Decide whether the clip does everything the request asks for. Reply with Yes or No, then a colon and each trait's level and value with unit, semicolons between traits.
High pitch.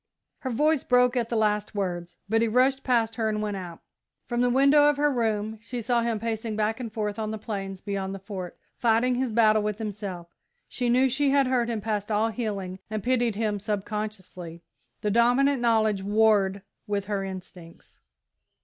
Yes: high, 220 Hz